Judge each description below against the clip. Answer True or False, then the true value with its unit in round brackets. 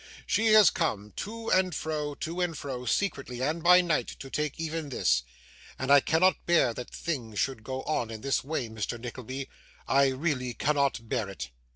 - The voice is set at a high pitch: False (140 Hz)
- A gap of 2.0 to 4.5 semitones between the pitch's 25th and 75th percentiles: False (4.9 semitones)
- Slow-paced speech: False (185 wpm)